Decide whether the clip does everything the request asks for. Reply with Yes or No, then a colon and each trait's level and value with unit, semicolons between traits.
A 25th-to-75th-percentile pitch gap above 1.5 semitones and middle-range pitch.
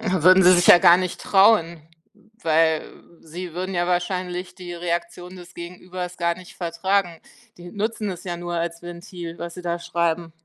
No: narrow, 1.2 semitones; medium, 175 Hz